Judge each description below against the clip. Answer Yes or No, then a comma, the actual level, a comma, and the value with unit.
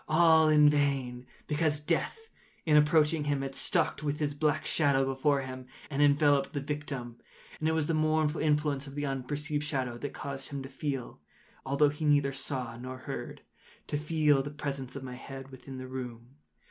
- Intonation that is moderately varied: No, narrow, 2.0 semitones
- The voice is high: No, medium, 145 Hz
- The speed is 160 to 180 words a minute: Yes, average, 175 wpm